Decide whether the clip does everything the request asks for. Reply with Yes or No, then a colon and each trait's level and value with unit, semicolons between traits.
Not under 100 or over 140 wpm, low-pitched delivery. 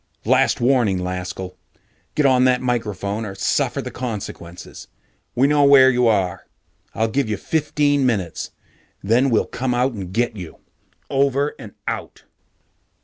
Yes: slow, 135 wpm; low, 120 Hz